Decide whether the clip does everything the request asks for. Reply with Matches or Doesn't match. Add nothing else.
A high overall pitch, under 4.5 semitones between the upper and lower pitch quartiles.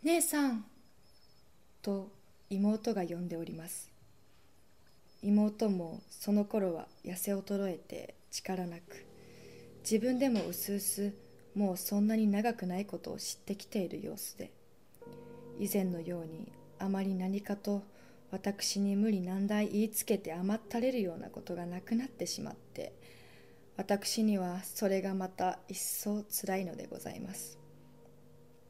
Matches